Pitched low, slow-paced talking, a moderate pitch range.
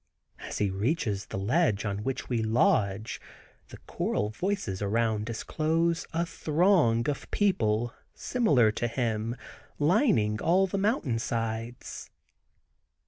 No: low, 115 Hz; slow, 120 wpm; wide, 7.4 semitones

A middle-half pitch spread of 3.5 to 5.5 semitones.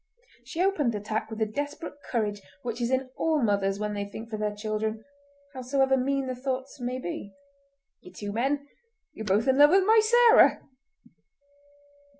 Yes: average, 4.7 semitones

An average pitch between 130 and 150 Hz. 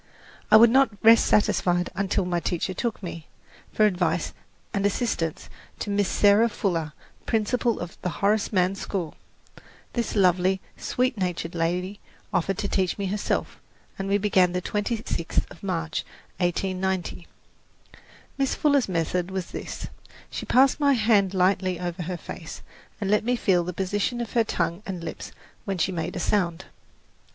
No: high, 190 Hz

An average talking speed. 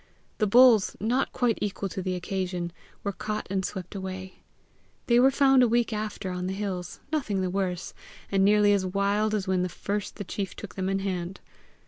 Yes: average, 190 wpm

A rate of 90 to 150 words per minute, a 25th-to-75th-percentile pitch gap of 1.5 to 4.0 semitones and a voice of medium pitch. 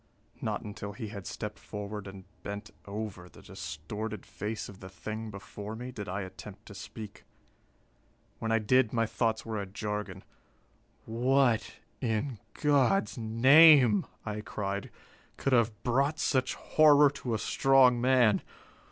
No: average, 145 wpm; average, 3.6 semitones; low, 110 Hz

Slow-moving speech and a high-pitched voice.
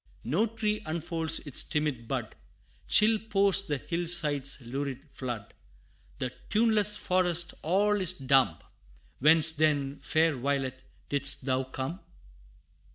No: slow, 120 wpm; medium, 155 Hz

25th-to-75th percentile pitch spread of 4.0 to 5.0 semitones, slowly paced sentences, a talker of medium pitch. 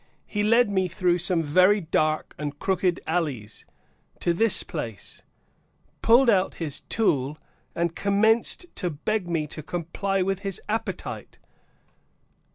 Yes: average, 4.6 semitones; slow, 130 wpm; medium, 180 Hz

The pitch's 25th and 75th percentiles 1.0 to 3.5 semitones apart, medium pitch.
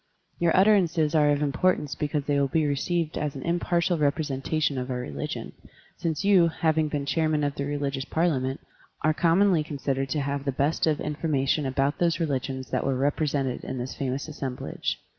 Yes: average, 2.8 semitones; medium, 145 Hz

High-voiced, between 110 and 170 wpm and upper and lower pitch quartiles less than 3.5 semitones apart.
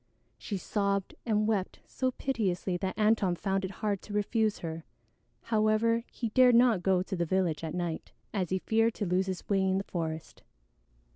No: high, 195 Hz; average, 185 wpm; average, 3.1 semitones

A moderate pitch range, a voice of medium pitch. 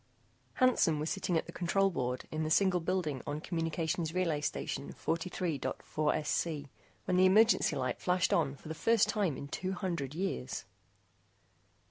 Yes: average, 3.6 semitones; medium, 165 Hz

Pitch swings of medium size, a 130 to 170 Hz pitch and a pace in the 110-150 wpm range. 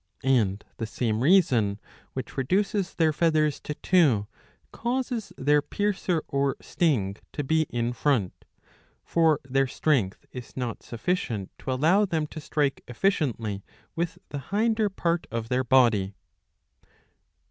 No: wide, 6.3 semitones; medium, 140 Hz; slow, 135 wpm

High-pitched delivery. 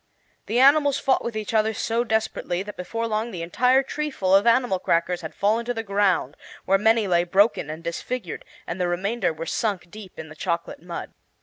Yes: high, 205 Hz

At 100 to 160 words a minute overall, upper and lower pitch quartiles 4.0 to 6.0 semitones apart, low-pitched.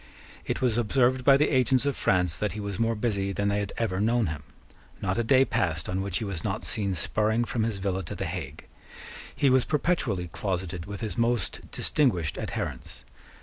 No: average, 200 wpm; average, 4.3 semitones; low, 105 Hz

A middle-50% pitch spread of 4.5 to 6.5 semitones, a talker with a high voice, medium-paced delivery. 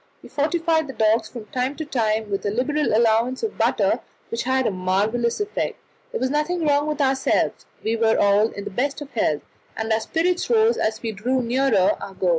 No: average, 5.2 semitones; high, 245 Hz; fast, 210 wpm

